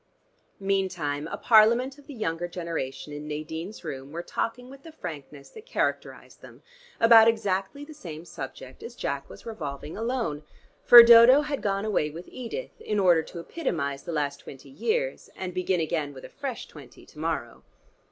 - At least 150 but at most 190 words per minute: Yes, average, 170 wpm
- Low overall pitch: No, medium, 180 Hz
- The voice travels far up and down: Yes, wide, 7.6 semitones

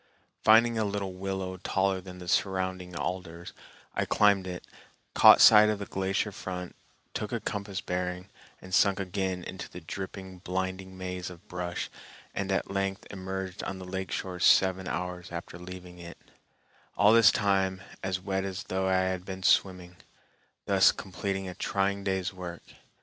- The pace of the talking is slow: No, average, 160 wpm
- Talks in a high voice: No, very low, 95 Hz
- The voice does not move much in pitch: Yes, narrow, 1.2 semitones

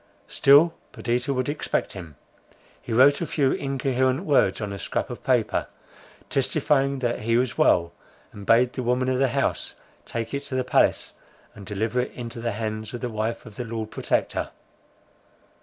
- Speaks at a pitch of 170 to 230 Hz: No, low, 125 Hz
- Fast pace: No, average, 175 wpm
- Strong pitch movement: No, average, 3.2 semitones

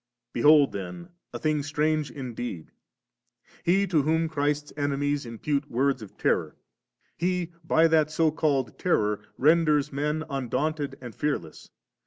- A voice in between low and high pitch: Yes, medium, 145 Hz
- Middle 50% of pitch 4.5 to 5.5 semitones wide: No, average, 2.8 semitones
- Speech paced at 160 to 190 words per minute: No, average, 145 wpm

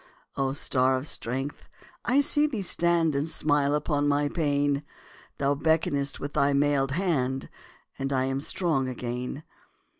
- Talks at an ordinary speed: Yes, average, 145 wpm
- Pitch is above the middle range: No, medium, 145 Hz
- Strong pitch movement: No, average, 2.7 semitones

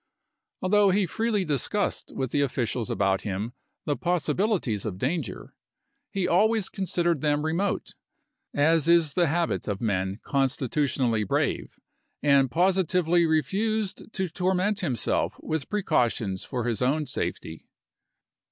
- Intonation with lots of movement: Yes, wide, 7.0 semitones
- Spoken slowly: Yes, slow, 130 wpm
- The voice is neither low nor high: Yes, medium, 155 Hz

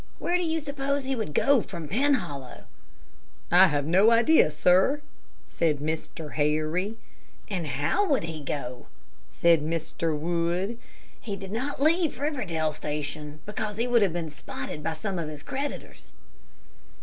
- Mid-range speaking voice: Yes, medium, 175 Hz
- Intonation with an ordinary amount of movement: No, wide, 8.2 semitones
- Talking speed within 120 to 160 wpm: Yes, average, 150 wpm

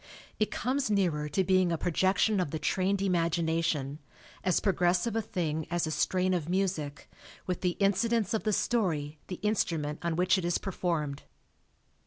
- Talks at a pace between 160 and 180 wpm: Yes, average, 170 wpm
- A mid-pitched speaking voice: Yes, medium, 180 Hz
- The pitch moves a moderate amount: Yes, average, 3.3 semitones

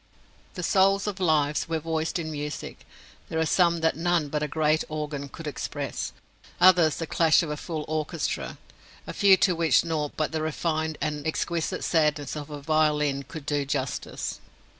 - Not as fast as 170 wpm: No, average, 180 wpm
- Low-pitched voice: No, medium, 155 Hz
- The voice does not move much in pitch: Yes, narrow, 1.9 semitones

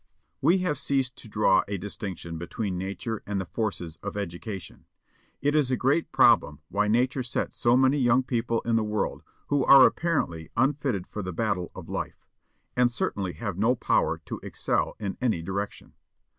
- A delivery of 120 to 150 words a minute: No, average, 175 wpm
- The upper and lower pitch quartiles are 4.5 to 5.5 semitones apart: Yes, average, 5.0 semitones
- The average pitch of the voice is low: Yes, low, 110 Hz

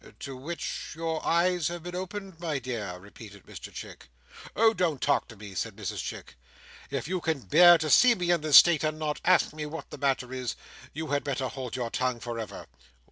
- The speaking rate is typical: No, fast, 210 wpm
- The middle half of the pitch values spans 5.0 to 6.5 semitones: Yes, average, 5.3 semitones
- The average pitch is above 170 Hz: No, medium, 150 Hz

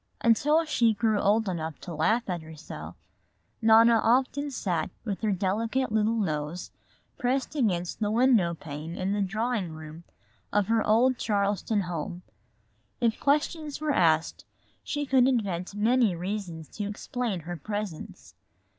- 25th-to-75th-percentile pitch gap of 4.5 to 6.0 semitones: Yes, average, 5.3 semitones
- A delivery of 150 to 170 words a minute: No, average, 140 wpm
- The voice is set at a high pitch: Yes, high, 210 Hz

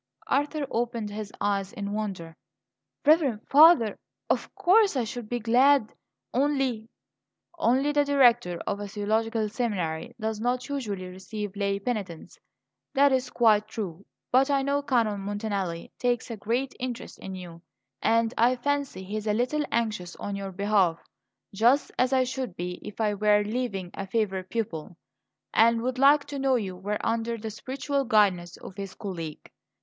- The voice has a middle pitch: No, high, 220 Hz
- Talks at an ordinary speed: Yes, average, 165 wpm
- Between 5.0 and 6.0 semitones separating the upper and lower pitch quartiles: No, average, 4.3 semitones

